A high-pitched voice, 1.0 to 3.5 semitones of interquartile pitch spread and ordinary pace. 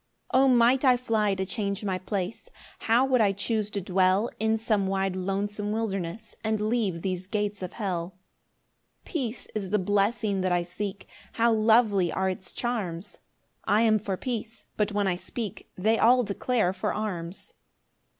Yes: high, 205 Hz; average, 2.9 semitones; average, 170 wpm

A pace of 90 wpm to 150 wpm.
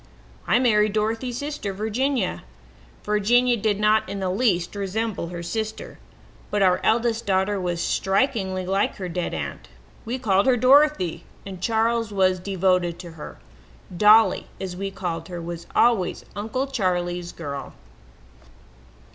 Yes: average, 140 wpm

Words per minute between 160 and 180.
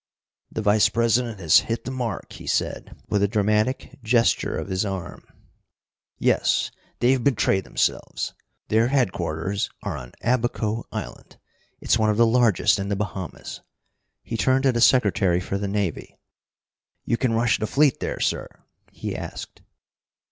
No: average, 150 wpm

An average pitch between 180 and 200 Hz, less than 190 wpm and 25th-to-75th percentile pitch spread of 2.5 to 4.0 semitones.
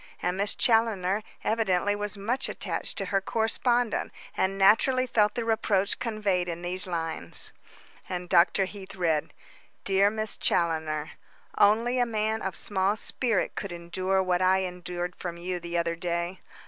Yes: high, 190 Hz; average, 150 wpm; average, 3.4 semitones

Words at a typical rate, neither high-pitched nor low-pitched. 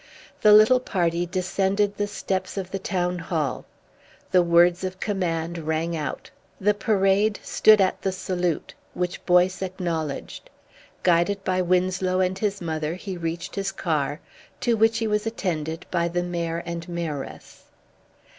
Yes: average, 145 wpm; medium, 180 Hz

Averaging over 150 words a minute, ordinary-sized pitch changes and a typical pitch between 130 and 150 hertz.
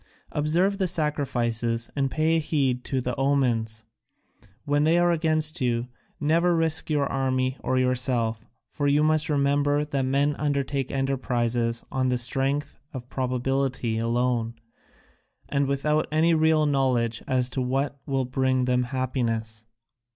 No: slow, 135 wpm; average, 3.0 semitones; low, 135 Hz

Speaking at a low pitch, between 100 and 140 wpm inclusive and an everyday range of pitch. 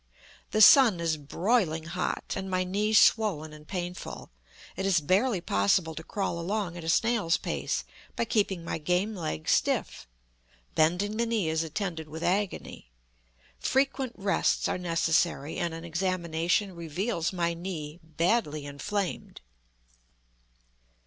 No: medium, 175 Hz; slow, 135 wpm; average, 3.9 semitones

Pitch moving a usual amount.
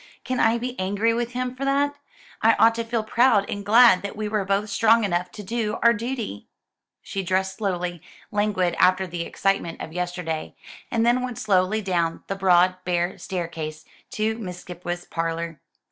Yes: average, 4.3 semitones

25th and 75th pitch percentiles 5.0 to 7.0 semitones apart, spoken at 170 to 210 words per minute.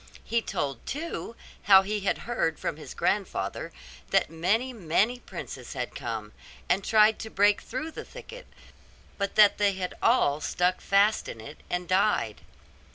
No: wide, 5.4 semitones; average, 160 wpm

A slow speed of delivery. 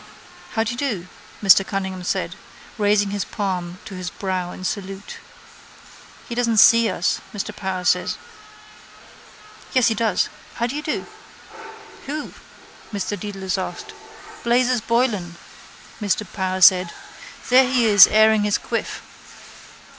Yes: slow, 130 wpm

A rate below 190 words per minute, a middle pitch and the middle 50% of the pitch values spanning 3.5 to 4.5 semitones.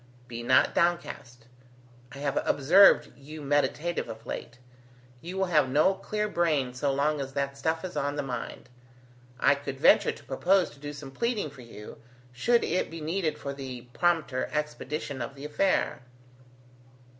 Yes: average, 165 wpm; medium, 145 Hz; average, 4.2 semitones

